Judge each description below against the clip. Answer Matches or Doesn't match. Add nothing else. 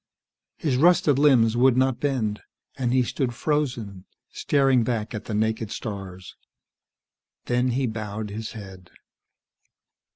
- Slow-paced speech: Matches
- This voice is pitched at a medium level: Doesn't match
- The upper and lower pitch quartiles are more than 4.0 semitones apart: Doesn't match